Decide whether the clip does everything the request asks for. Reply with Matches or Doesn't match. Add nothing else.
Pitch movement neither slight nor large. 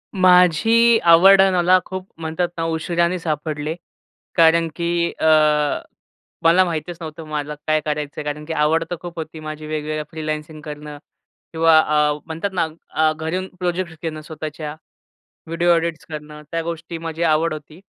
Doesn't match